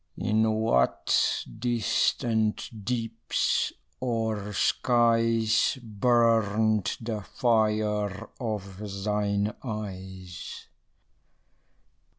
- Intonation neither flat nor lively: No, narrow, 1.8 semitones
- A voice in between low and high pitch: No, low, 110 Hz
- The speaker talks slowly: Yes, slow, 60 wpm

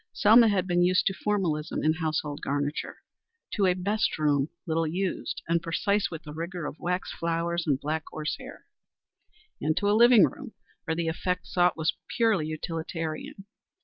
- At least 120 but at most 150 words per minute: No, average, 170 wpm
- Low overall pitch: No, medium, 170 Hz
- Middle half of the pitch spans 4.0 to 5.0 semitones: No, average, 3.4 semitones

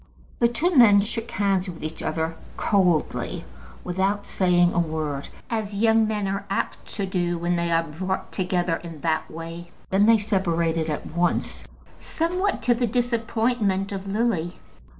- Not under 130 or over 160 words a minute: Yes, average, 155 wpm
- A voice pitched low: No, high, 190 Hz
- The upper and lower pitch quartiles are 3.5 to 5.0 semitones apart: Yes, average, 4.5 semitones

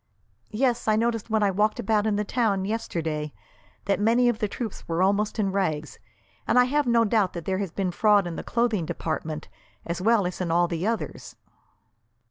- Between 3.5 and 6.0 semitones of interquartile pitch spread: Yes, average, 4.4 semitones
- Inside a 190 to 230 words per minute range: Yes, average, 195 wpm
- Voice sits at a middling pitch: No, high, 205 Hz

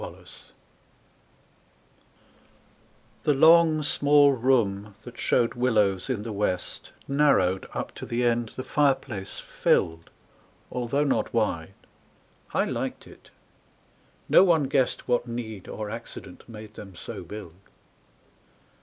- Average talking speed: No, slow, 120 wpm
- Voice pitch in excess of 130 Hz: No, low, 120 Hz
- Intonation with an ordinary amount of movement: Yes, average, 4.8 semitones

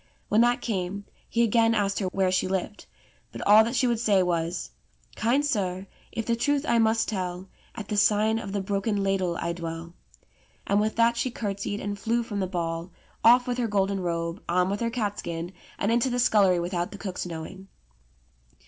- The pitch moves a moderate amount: Yes, average, 3.9 semitones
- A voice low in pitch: No, high, 200 Hz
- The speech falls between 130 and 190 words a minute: No, average, 200 wpm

